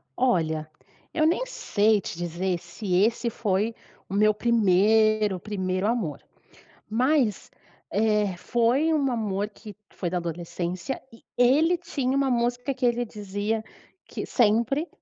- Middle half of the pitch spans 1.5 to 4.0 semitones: No, average, 4.5 semitones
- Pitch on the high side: Yes, high, 215 Hz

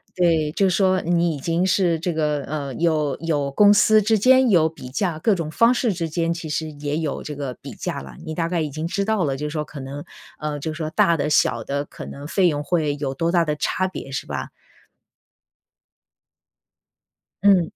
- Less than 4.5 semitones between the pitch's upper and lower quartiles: Yes, average, 3.4 semitones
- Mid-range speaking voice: Yes, medium, 160 Hz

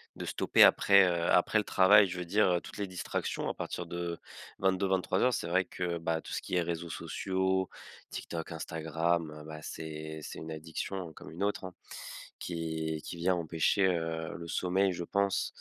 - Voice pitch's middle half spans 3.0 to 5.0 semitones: No, narrow, 2.5 semitones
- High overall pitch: No, very low, 85 Hz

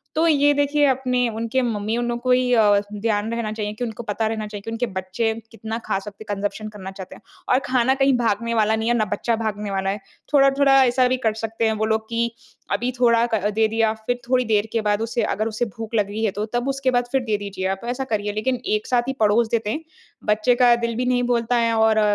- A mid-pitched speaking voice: No, high, 225 Hz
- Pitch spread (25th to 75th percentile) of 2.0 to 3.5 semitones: Yes, narrow, 2.6 semitones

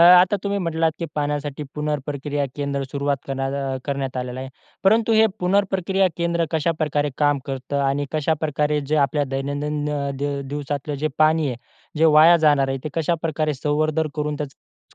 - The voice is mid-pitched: Yes, medium, 150 Hz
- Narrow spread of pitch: Yes, narrow, 2.2 semitones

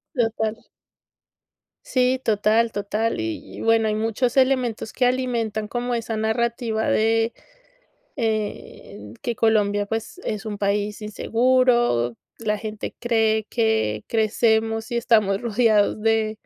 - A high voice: Yes, high, 220 Hz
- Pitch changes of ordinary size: No, narrow, 1.8 semitones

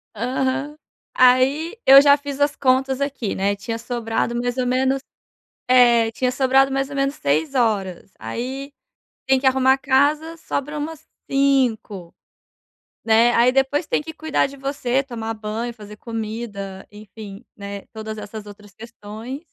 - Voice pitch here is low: No, very high, 250 Hz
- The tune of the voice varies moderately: Yes, average, 3.9 semitones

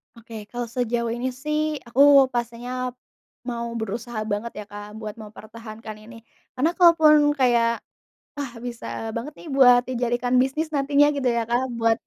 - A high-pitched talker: Yes, high, 240 Hz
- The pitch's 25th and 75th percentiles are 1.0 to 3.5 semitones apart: Yes, average, 2.9 semitones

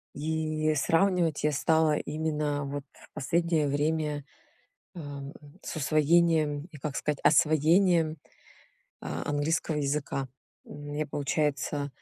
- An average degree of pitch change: No, narrow, 1.6 semitones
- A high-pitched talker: No, medium, 150 Hz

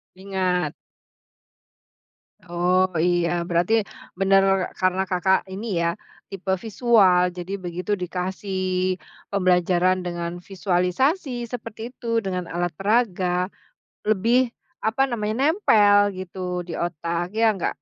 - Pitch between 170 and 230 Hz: Yes, medium, 185 Hz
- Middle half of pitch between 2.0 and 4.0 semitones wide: Yes, average, 3.0 semitones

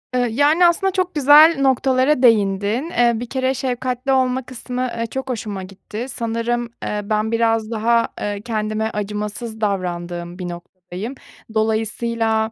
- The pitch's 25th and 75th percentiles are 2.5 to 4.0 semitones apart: Yes, average, 3.4 semitones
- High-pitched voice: Yes, high, 230 Hz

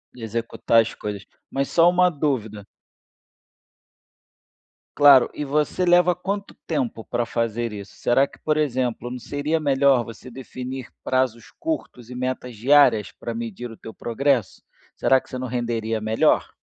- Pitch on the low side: Yes, low, 125 Hz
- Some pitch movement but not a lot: Yes, average, 3.9 semitones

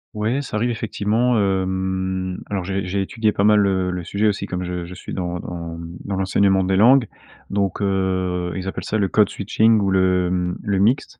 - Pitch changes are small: Yes, narrow, 2.3 semitones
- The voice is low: Yes, very low, 95 Hz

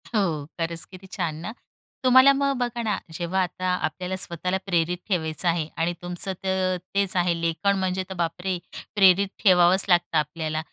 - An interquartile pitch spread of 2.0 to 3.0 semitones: Yes, narrow, 2.4 semitones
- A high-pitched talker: No, medium, 180 Hz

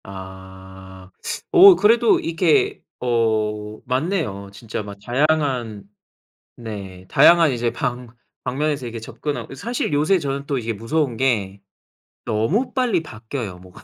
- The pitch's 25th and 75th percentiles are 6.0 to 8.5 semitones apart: Yes, wide, 7.0 semitones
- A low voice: Yes, low, 120 Hz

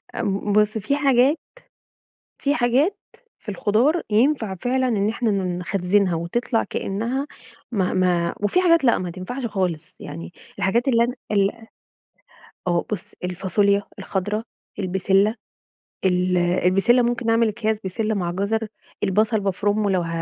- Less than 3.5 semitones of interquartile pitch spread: No, average, 4.2 semitones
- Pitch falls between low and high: No, high, 205 Hz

